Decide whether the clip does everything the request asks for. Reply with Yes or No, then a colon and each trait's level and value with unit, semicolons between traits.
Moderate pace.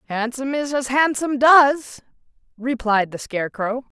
No: slow, 120 wpm